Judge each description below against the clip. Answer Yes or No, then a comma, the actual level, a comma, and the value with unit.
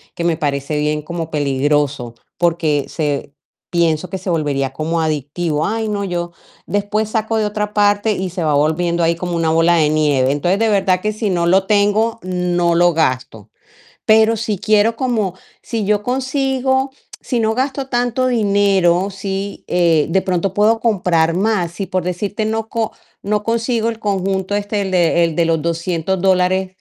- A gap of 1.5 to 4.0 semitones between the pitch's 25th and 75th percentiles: No, average, 4.4 semitones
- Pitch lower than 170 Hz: No, medium, 185 Hz